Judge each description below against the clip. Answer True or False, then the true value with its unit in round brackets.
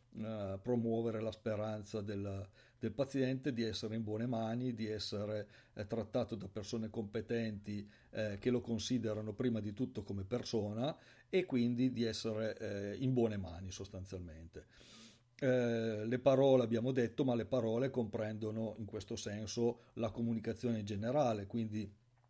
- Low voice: True (115 Hz)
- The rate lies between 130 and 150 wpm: True (145 wpm)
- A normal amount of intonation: False (2.2 semitones)